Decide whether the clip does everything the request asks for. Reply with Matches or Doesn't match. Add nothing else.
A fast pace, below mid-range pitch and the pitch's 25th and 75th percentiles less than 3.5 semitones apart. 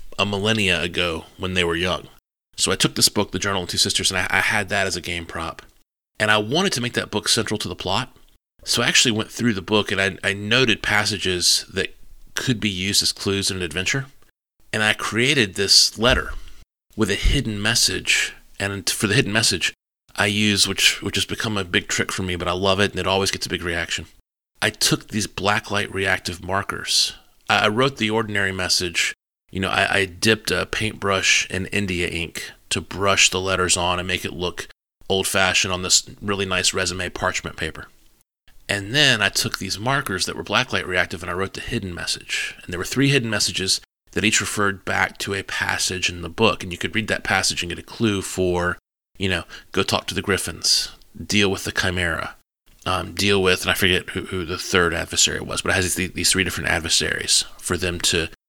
Matches